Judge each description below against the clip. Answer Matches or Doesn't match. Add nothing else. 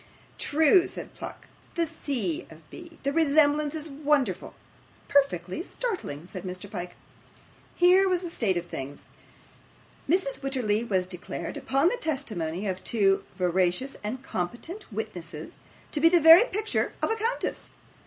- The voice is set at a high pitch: Matches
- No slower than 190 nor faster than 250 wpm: Doesn't match